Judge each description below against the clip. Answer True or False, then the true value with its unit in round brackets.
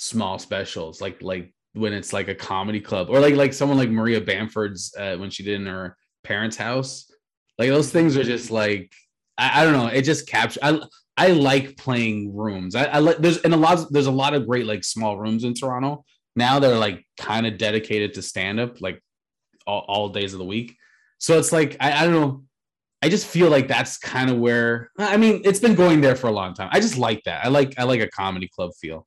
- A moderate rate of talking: False (235 wpm)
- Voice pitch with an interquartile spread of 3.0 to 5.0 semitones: False (5.6 semitones)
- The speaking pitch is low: True (120 Hz)